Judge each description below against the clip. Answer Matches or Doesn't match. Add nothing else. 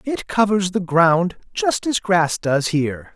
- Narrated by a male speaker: Matches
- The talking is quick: Doesn't match